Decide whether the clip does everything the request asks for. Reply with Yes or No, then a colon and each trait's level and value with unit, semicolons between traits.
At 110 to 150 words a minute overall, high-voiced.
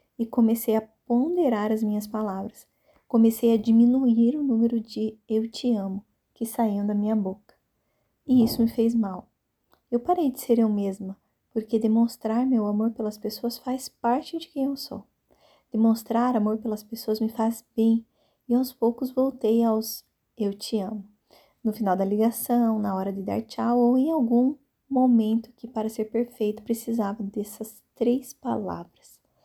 No: average, 165 wpm; high, 230 Hz